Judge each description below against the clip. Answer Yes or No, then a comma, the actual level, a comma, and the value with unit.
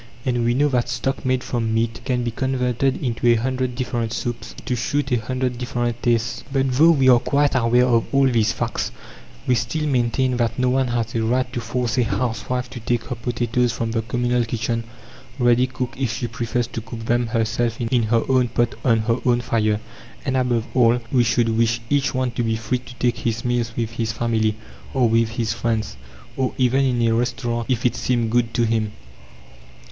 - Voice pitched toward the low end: Yes, low, 120 Hz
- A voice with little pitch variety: Yes, narrow, 1.6 semitones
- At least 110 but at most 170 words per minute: No, fast, 205 wpm